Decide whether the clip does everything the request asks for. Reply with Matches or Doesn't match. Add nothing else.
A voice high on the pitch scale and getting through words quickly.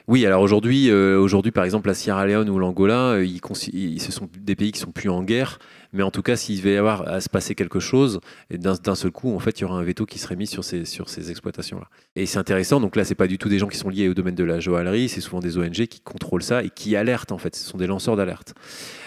Doesn't match